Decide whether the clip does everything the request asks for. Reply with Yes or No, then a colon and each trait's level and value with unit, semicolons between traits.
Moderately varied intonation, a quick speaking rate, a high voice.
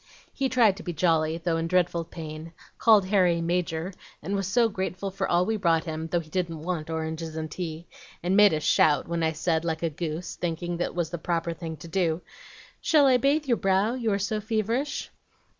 No: average, 3.5 semitones; fast, 210 wpm; medium, 175 Hz